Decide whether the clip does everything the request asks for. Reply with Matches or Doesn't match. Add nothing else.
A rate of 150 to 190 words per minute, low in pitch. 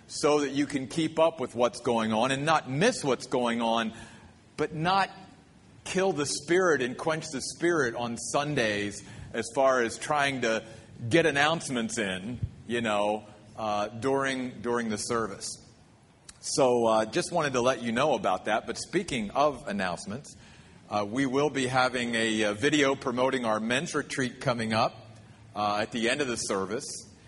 Matches